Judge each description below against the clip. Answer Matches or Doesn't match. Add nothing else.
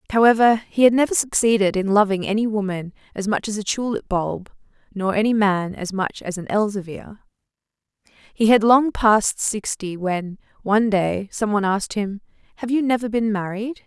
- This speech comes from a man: Doesn't match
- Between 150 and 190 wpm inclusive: Matches